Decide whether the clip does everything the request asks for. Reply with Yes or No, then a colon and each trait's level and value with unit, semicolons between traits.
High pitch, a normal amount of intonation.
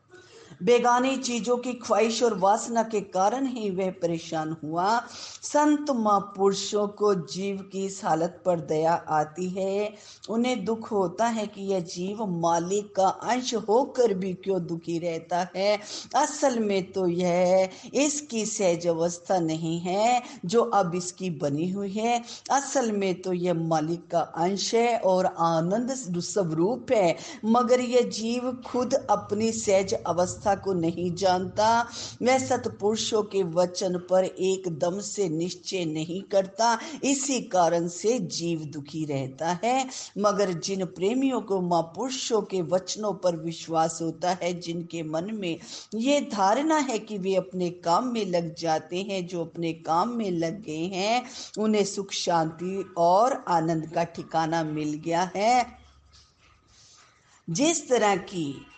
Yes: high, 195 Hz; average, 4.6 semitones